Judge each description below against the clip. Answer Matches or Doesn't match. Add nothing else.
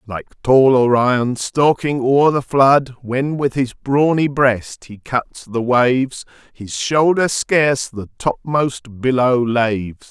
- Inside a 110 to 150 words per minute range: Matches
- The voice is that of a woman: Doesn't match